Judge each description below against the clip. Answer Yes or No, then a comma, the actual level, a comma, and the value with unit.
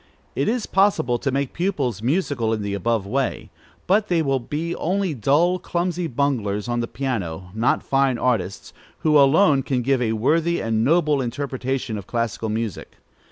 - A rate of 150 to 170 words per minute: Yes, average, 165 wpm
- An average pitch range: No, wide, 5.8 semitones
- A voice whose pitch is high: No, low, 135 Hz